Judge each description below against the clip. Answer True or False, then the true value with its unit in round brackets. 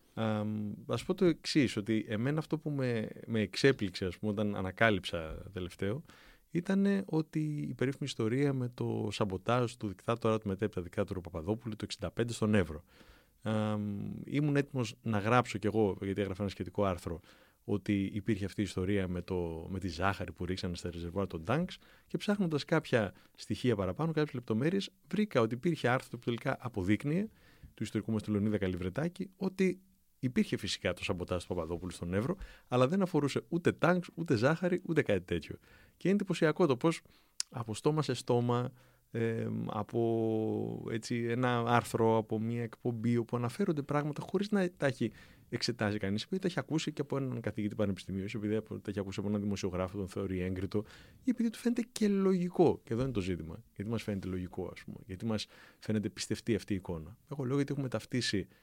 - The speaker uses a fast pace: True (180 wpm)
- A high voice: False (115 Hz)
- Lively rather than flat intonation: True (5.8 semitones)